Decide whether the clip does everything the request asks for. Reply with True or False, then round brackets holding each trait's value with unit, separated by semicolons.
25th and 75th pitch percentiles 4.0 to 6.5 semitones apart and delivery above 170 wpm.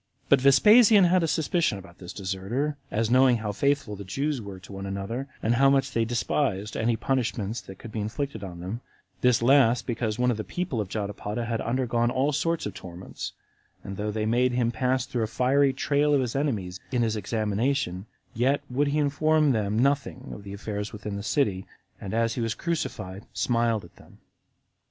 True (4.9 semitones; 200 wpm)